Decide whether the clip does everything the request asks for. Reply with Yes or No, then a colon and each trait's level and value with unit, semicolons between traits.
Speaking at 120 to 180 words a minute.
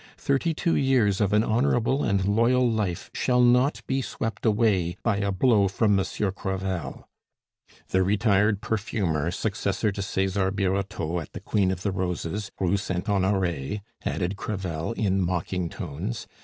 Yes: average, 155 wpm